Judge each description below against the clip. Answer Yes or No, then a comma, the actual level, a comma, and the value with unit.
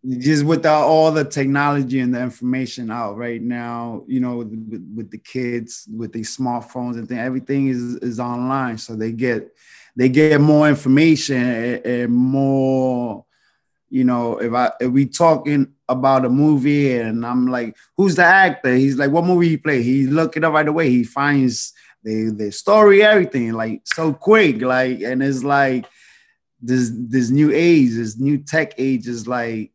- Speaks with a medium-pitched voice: No, low, 130 Hz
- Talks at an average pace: Yes, average, 175 wpm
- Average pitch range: Yes, average, 3.1 semitones